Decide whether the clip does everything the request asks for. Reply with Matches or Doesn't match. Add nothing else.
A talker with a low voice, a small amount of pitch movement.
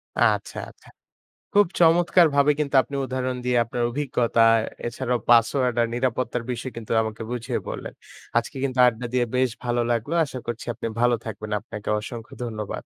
Matches